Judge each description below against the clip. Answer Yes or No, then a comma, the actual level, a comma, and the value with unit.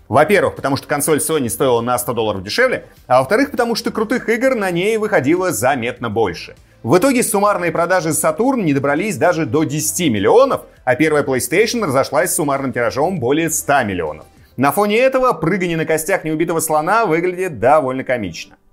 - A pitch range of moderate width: No, wide, 7.2 semitones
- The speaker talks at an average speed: No, fast, 170 wpm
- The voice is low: No, medium, 160 Hz